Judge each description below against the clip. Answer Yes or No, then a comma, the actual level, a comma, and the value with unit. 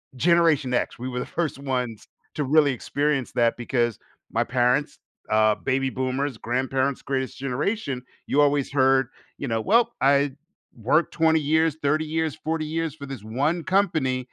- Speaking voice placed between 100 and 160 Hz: Yes, low, 135 Hz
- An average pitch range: Yes, average, 3.6 semitones